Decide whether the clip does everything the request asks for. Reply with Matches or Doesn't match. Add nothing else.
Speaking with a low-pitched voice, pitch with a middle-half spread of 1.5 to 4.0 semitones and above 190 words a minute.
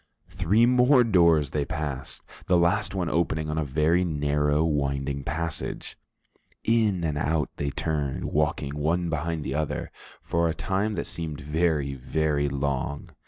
Doesn't match